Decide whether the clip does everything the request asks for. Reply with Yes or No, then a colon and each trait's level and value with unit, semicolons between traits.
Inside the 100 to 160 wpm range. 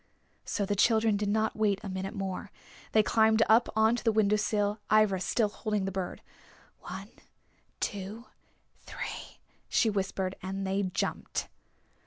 Yes: average, 145 wpm